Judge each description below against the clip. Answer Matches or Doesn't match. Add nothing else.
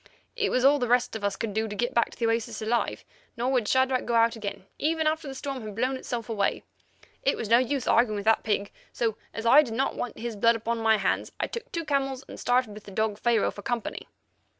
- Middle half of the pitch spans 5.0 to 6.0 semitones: Doesn't match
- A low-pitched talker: Doesn't match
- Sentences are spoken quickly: Matches